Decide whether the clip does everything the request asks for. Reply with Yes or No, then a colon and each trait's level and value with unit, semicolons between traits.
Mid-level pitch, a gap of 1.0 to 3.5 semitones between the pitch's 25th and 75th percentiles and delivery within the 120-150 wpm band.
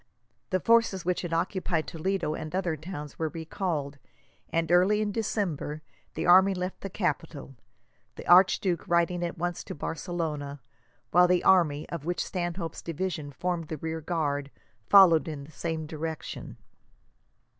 Yes: medium, 170 Hz; average, 2.8 semitones; average, 145 wpm